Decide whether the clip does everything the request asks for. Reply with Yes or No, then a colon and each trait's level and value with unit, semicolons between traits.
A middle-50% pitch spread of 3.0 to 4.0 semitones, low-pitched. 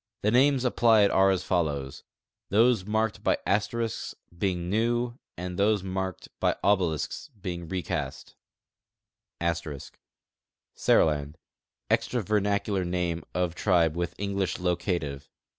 Yes: average, 3.5 semitones; very low, 95 Hz